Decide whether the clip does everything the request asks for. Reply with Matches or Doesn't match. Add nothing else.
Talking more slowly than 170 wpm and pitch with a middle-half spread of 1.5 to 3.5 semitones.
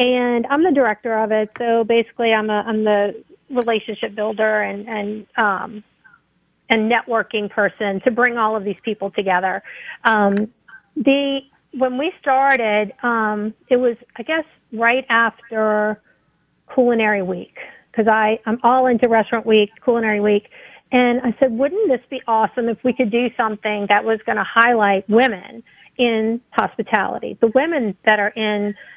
Matches